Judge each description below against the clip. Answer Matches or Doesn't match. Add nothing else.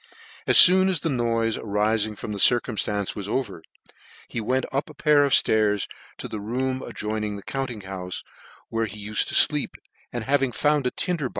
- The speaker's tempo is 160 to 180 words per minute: Doesn't match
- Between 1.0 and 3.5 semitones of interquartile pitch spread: Doesn't match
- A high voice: Doesn't match